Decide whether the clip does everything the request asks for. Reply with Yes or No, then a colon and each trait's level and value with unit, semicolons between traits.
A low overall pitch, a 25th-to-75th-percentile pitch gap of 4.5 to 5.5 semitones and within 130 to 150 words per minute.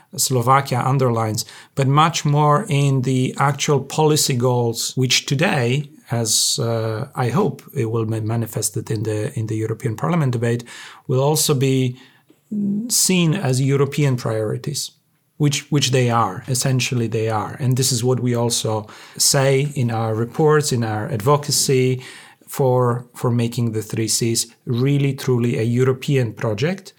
No: low, 130 Hz; average, 3.5 semitones; average, 145 wpm